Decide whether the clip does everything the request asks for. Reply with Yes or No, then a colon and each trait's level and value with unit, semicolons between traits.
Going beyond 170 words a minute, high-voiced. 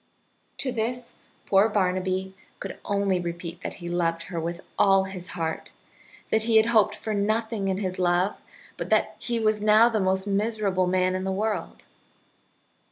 No: average, 165 wpm; high, 195 Hz